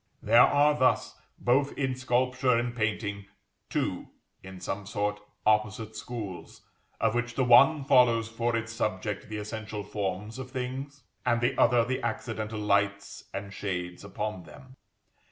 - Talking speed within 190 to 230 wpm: No, average, 145 wpm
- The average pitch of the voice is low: Yes, low, 115 Hz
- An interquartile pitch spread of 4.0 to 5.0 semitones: No, average, 3.4 semitones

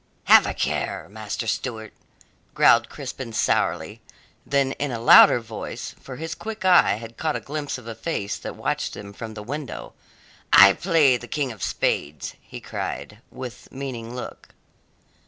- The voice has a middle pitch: No, low, 120 Hz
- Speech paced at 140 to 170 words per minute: Yes, average, 160 wpm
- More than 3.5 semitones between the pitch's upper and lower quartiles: Yes, average, 4.5 semitones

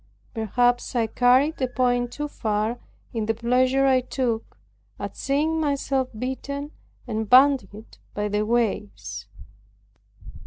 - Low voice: No, high, 245 Hz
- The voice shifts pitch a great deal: No, average, 3.4 semitones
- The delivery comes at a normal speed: No, slow, 120 wpm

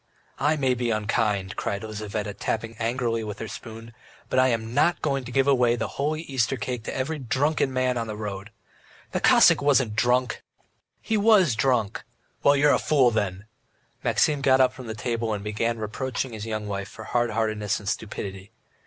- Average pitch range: Yes, average, 3.6 semitones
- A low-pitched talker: Yes, low, 115 Hz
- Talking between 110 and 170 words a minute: No, average, 190 wpm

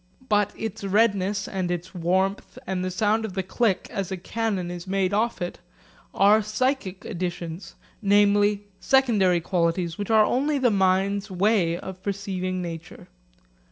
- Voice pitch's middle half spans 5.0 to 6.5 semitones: No, narrow, 2.4 semitones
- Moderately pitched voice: No, high, 195 Hz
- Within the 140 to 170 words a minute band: Yes, average, 150 wpm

